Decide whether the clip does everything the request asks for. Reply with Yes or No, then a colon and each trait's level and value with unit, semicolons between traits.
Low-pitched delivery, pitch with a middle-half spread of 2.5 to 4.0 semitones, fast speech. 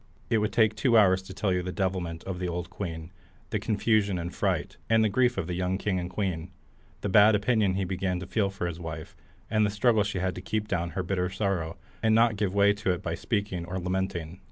Yes: very low, 95 Hz; average, 2.8 semitones; fast, 235 wpm